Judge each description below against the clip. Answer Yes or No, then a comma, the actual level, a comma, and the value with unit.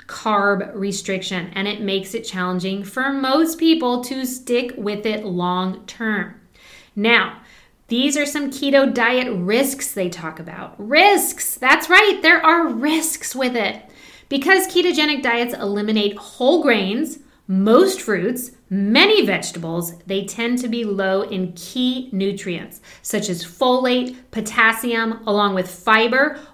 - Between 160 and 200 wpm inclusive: No, slow, 135 wpm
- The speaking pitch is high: Yes, high, 230 Hz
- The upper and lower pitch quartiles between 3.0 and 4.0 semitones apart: No, wide, 5.5 semitones